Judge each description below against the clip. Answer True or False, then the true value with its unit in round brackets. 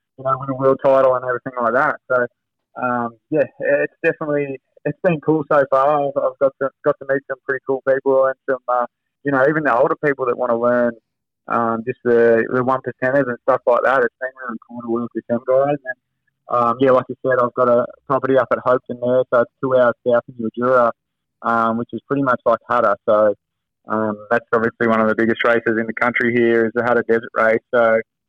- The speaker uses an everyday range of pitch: False (2.3 semitones)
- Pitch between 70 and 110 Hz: False (125 Hz)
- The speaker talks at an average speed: False (235 wpm)